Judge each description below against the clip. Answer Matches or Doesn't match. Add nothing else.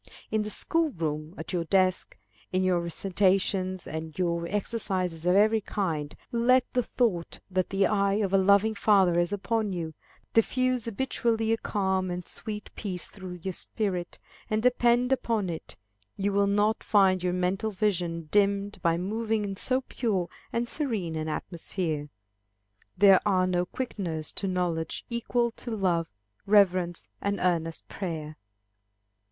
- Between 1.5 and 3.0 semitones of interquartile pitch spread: Doesn't match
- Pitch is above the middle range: Matches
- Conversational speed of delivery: Matches